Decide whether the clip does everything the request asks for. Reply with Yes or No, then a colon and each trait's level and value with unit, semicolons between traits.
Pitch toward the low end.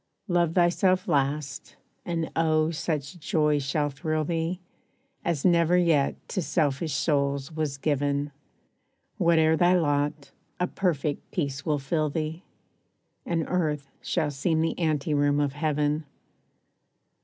No: medium, 155 Hz